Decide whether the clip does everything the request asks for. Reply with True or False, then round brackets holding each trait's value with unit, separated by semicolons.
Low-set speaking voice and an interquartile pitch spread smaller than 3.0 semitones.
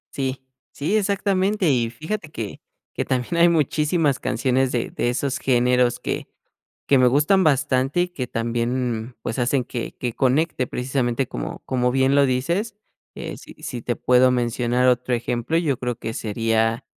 False (130 Hz; 3.3 semitones)